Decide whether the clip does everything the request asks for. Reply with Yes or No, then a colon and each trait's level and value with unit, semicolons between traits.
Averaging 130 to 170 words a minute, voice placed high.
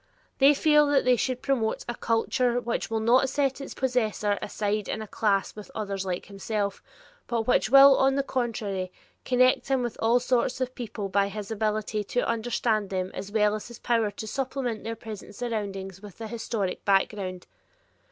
No: average, 185 wpm; high, 225 Hz